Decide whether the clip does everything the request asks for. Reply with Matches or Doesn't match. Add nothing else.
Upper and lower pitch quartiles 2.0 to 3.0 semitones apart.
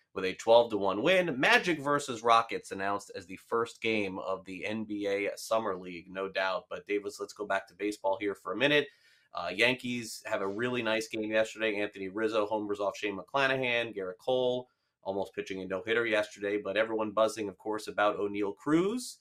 Doesn't match